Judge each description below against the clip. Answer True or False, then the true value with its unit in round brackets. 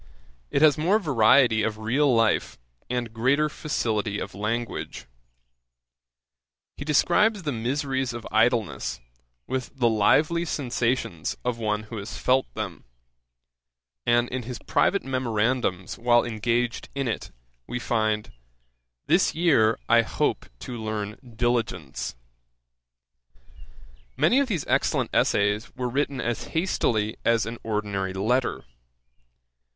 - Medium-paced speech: False (120 wpm)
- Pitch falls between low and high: False (120 Hz)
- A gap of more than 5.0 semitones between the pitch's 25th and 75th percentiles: False (3.5 semitones)